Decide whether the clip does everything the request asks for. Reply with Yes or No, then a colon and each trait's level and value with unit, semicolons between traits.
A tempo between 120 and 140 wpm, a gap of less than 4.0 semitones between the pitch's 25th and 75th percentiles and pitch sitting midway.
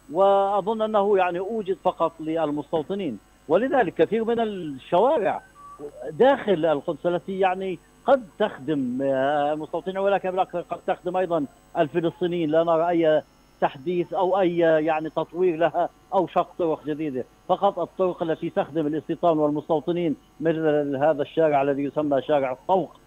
Yes: average, 125 wpm; average, 3.4 semitones; medium, 170 Hz